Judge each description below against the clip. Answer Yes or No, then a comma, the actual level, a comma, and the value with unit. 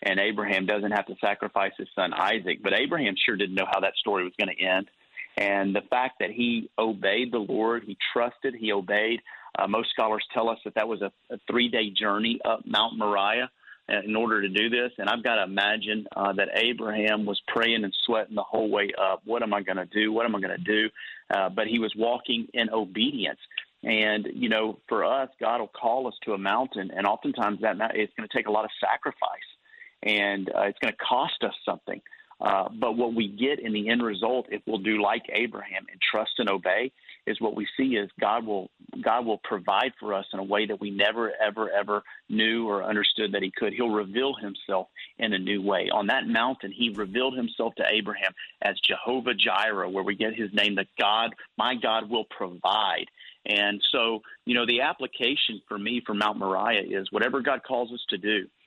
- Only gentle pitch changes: Yes, narrow, 2.2 semitones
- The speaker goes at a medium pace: No, fast, 215 wpm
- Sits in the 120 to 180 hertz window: No, low, 105 Hz